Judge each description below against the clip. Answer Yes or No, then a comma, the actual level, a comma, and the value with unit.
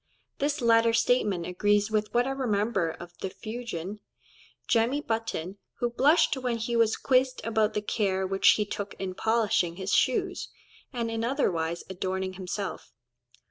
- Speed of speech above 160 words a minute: No, average, 150 wpm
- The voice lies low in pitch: No, high, 215 Hz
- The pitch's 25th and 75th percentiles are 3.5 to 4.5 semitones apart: Yes, average, 3.9 semitones